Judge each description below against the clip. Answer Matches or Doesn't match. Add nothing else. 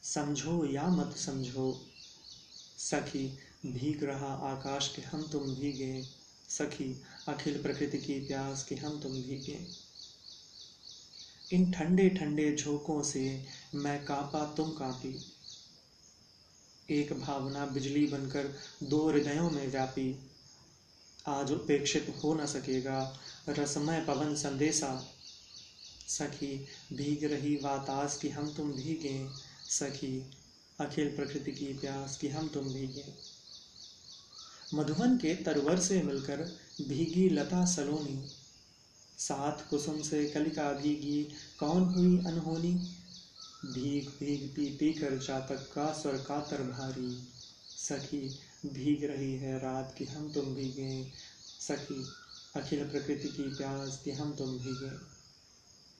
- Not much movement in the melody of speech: Matches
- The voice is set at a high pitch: Doesn't match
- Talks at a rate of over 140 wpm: Doesn't match